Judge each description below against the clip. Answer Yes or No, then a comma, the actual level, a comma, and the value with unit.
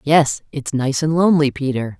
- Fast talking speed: No, average, 180 wpm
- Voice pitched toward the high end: No, medium, 140 Hz